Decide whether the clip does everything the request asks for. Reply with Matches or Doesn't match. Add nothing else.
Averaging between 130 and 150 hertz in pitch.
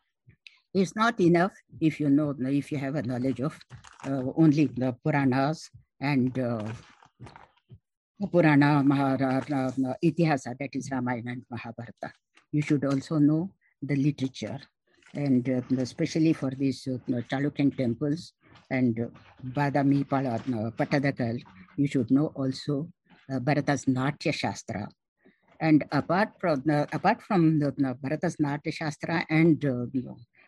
Matches